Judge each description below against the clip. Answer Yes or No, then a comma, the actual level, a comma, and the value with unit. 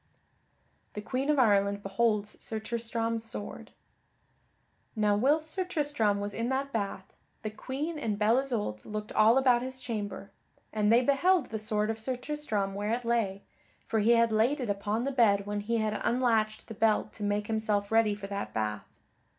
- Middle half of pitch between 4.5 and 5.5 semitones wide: No, average, 3.2 semitones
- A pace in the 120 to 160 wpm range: No, average, 185 wpm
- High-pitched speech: Yes, high, 220 Hz